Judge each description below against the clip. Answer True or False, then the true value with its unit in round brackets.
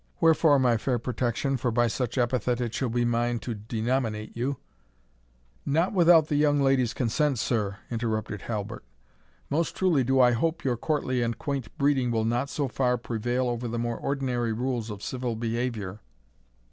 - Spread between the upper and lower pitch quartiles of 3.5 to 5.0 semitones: False (3.0 semitones)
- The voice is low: True (120 Hz)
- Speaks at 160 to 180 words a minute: True (170 wpm)